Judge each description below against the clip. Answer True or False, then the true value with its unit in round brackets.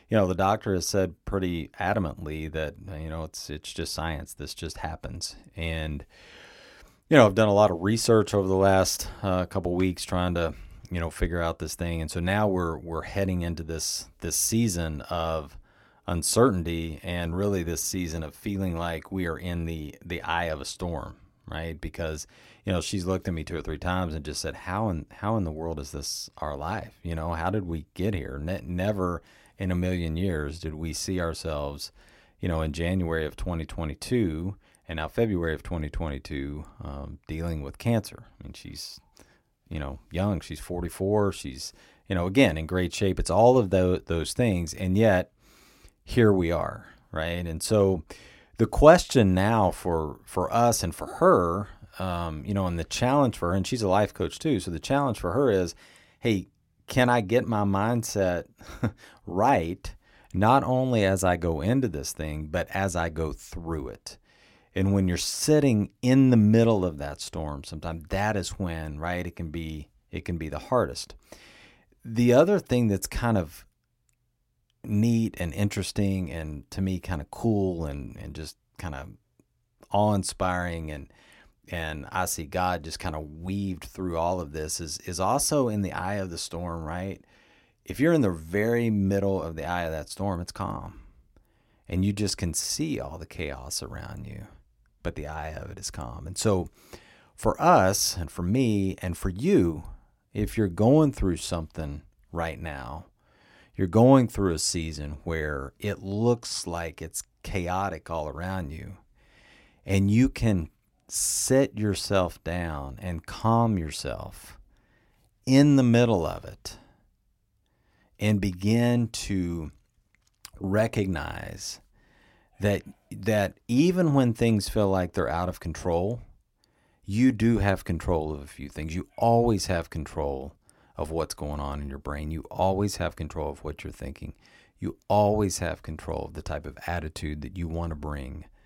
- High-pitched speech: False (90 Hz)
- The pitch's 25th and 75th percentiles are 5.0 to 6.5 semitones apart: False (4.1 semitones)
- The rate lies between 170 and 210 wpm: True (175 wpm)